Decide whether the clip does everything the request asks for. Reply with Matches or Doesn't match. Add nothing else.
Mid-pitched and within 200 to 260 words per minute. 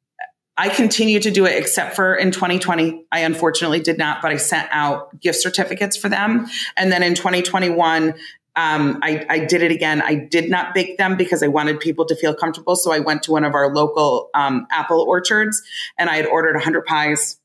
Matches